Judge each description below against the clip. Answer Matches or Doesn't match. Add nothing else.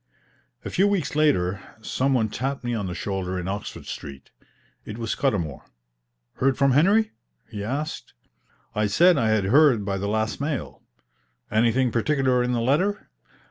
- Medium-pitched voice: Doesn't match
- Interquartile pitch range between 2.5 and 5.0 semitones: Doesn't match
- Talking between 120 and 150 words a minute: Doesn't match